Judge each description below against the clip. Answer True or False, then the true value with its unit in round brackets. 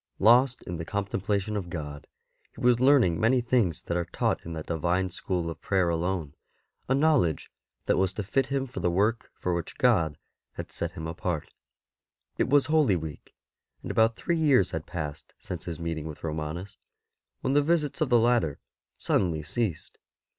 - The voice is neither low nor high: False (95 Hz)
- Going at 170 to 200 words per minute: True (180 wpm)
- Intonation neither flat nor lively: False (6.8 semitones)